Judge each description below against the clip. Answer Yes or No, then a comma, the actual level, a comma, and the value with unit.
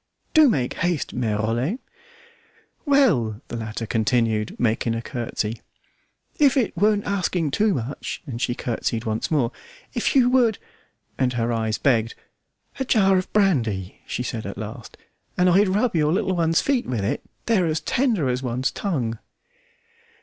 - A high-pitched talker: No, low, 135 Hz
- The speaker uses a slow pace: No, average, 155 wpm